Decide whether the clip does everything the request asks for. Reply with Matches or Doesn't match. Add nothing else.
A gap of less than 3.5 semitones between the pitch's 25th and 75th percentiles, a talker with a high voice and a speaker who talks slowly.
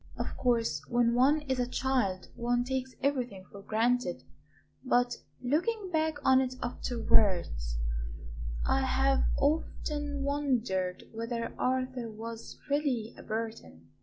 Matches